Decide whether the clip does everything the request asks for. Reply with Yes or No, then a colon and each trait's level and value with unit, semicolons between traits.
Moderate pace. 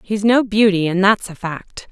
No: fast, 220 wpm